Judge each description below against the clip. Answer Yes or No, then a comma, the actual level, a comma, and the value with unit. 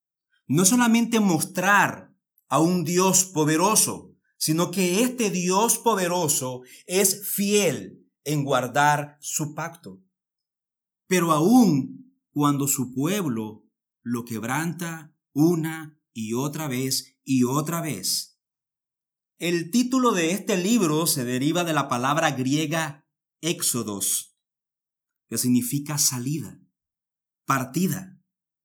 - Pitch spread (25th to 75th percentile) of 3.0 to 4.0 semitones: No, average, 4.7 semitones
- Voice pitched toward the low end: No, medium, 160 Hz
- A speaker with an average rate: No, slow, 100 wpm